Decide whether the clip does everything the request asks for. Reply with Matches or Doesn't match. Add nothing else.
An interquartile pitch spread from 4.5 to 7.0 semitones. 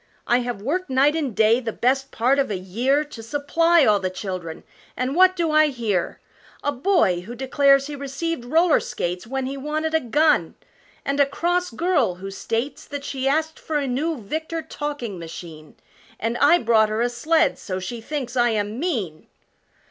Matches